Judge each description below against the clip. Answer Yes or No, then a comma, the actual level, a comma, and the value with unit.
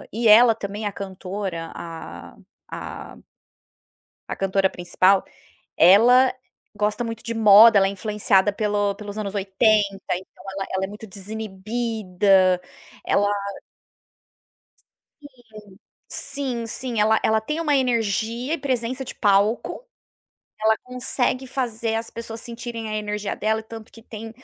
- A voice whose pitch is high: Yes, high, 215 Hz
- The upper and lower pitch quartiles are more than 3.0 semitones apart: No, average, 2.7 semitones